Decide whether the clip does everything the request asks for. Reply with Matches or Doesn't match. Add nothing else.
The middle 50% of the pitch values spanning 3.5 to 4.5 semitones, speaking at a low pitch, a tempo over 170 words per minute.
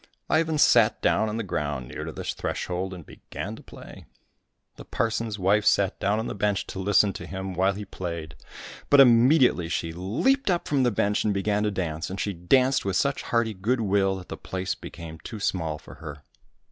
Matches